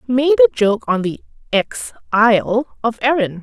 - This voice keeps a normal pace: Yes, average, 160 wpm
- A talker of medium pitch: No, high, 235 Hz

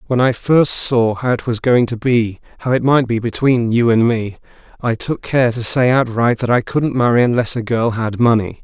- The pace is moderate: No, fast, 215 wpm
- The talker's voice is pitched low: Yes, low, 120 Hz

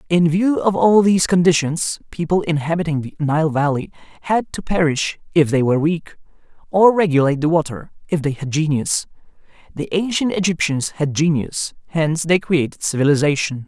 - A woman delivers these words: No, male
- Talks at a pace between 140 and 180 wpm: Yes, average, 155 wpm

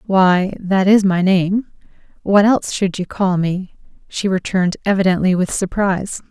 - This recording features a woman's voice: Yes, female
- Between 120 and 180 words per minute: Yes, average, 145 wpm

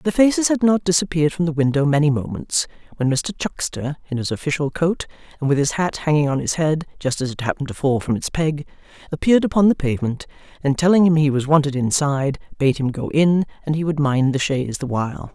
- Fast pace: Yes, fast, 225 wpm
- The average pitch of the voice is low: No, medium, 150 Hz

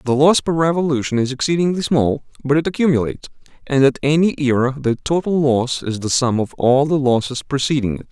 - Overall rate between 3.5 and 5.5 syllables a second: No, 5.8 syllables/s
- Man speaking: Yes, male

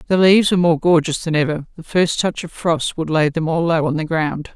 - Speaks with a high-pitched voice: No, medium, 165 Hz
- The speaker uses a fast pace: Yes, fast, 265 wpm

